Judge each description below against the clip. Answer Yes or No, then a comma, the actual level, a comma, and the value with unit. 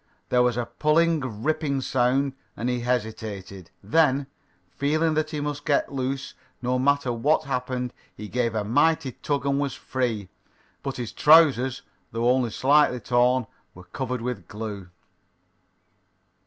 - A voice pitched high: No, low, 125 Hz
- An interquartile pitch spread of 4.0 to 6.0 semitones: No, average, 3.2 semitones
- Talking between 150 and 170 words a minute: No, average, 140 wpm